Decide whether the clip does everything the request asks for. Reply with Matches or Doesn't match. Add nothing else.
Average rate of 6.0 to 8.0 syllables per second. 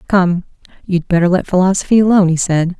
Matches